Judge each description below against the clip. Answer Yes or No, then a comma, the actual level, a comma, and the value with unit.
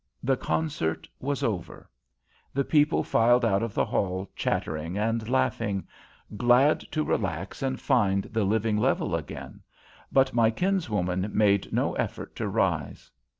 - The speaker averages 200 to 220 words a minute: No, average, 140 wpm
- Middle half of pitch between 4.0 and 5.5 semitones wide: Yes, average, 5.2 semitones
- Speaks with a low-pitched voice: Yes, low, 115 Hz